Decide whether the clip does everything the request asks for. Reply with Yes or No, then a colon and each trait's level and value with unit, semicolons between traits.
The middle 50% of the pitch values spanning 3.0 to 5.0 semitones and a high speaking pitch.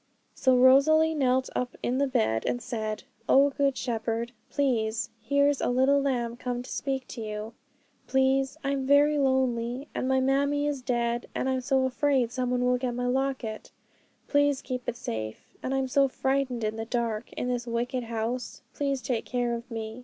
No: narrow, 2.4 semitones; very high, 255 Hz